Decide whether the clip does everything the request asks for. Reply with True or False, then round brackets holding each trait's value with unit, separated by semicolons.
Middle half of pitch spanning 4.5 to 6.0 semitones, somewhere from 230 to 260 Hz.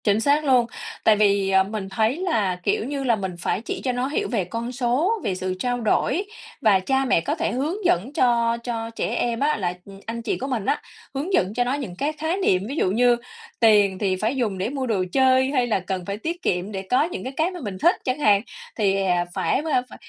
True (5.2 semitones; 235 Hz)